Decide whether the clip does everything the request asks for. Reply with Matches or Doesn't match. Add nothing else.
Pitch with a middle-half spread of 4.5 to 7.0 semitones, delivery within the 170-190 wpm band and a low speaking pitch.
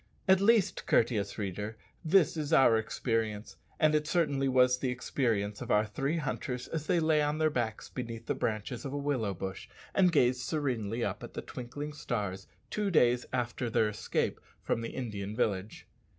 Matches